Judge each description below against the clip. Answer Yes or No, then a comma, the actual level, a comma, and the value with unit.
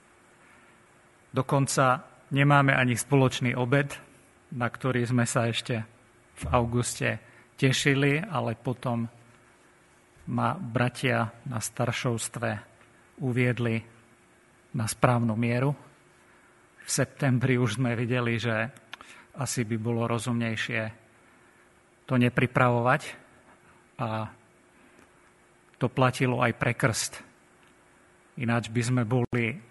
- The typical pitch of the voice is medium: No, low, 120 Hz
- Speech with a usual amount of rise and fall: No, narrow, 1.7 semitones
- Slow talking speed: Yes, slow, 90 wpm